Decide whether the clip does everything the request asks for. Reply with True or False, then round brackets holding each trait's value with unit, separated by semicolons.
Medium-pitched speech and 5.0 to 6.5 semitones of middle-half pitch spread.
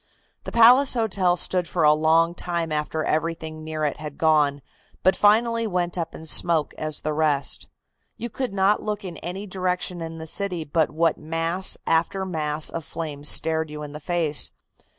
False (165 Hz; 3.1 semitones)